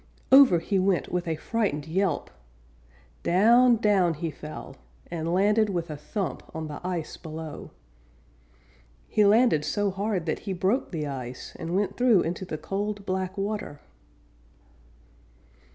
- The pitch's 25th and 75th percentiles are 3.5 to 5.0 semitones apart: Yes, average, 4.3 semitones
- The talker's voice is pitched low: No, medium, 185 Hz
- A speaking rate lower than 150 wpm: Yes, average, 140 wpm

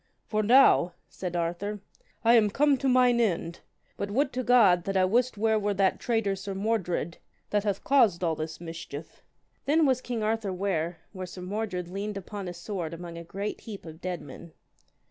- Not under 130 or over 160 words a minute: No, average, 190 wpm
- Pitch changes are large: No, average, 4.2 semitones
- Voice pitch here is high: Yes, high, 200 Hz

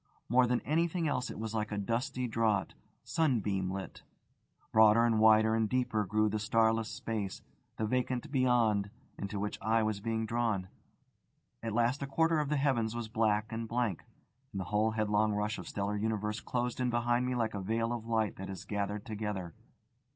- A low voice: Yes, low, 110 Hz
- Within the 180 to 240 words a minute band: Yes, average, 185 wpm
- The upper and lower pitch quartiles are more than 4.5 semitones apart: No, narrow, 2.5 semitones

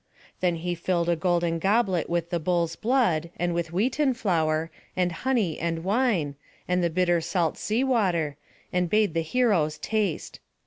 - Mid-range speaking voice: Yes, medium, 175 Hz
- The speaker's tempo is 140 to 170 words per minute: Yes, average, 165 wpm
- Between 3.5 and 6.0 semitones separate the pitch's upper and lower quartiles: Yes, average, 3.9 semitones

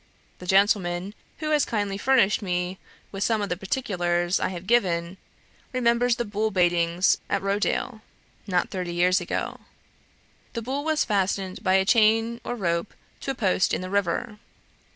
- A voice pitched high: Yes, high, 195 Hz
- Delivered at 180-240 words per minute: No, average, 160 wpm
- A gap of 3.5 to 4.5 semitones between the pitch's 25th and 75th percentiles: Yes, average, 3.9 semitones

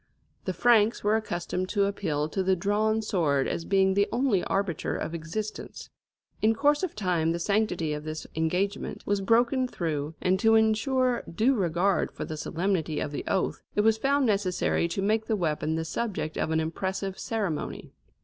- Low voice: No, high, 195 Hz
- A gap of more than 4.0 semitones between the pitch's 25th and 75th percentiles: Yes, average, 4.9 semitones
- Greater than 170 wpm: Yes, average, 180 wpm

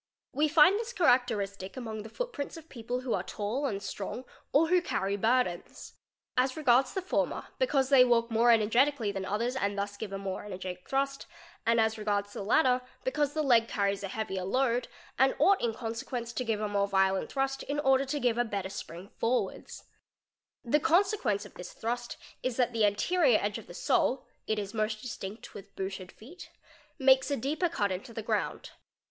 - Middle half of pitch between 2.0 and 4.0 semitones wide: No, average, 5.0 semitones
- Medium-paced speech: Yes, average, 190 wpm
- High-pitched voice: Yes, high, 235 Hz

